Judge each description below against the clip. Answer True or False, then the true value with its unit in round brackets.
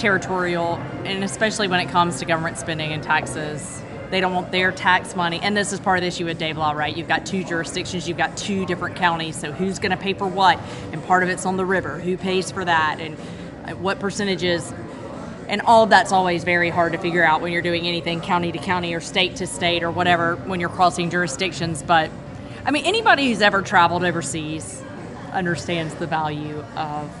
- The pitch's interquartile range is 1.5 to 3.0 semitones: True (2.5 semitones)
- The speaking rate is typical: False (215 wpm)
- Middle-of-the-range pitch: True (175 Hz)